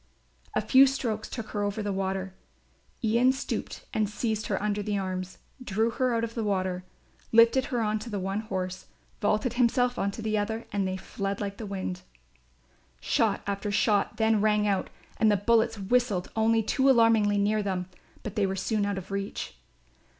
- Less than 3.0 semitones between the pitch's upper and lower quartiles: Yes, narrow, 2.4 semitones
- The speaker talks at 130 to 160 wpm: No, average, 185 wpm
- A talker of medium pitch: No, high, 210 Hz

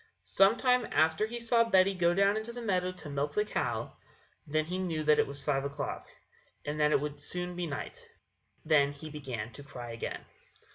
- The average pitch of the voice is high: No, medium, 160 Hz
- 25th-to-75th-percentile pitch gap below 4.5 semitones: No, average, 5.2 semitones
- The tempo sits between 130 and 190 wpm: No, average, 200 wpm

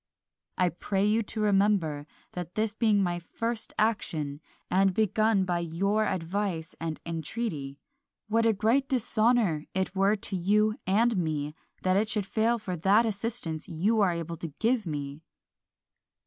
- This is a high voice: Yes, high, 195 Hz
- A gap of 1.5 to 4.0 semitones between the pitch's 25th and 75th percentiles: No, average, 4.5 semitones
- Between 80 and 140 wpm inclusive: No, average, 150 wpm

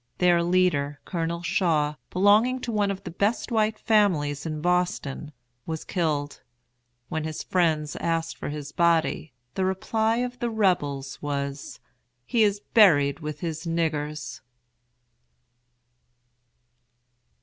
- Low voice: No, medium, 170 Hz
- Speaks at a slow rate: Yes, slow, 120 wpm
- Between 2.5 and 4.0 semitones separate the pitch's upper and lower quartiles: No, average, 4.8 semitones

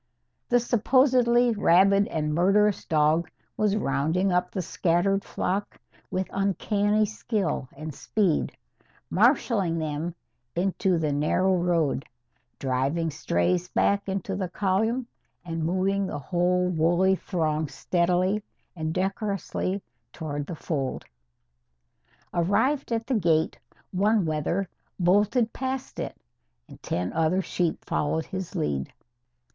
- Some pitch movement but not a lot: Yes, average, 3.9 semitones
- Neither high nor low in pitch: Yes, medium, 180 Hz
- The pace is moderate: No, slow, 115 wpm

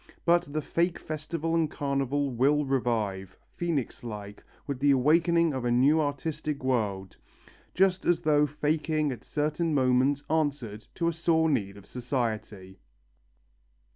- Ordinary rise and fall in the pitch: Yes, average, 4.4 semitones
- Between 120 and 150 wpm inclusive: Yes, average, 140 wpm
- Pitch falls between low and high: Yes, medium, 145 Hz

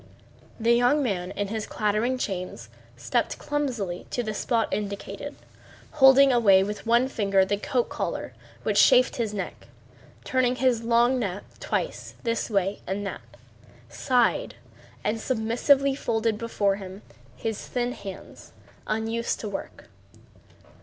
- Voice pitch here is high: Yes, high, 225 Hz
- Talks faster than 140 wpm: No, slow, 135 wpm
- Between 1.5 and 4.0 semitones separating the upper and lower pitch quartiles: Yes, average, 3.5 semitones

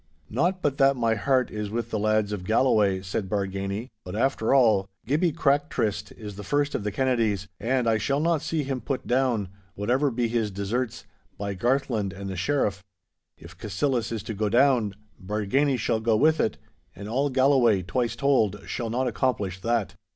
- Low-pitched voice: Yes, low, 115 Hz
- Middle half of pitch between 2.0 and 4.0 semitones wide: No, average, 4.6 semitones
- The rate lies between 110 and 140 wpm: No, average, 185 wpm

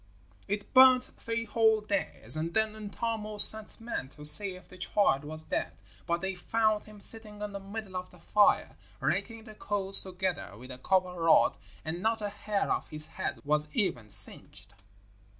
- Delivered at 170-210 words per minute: Yes, average, 180 wpm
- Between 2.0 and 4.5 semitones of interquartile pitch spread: Yes, average, 4.1 semitones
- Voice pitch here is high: Yes, high, 200 Hz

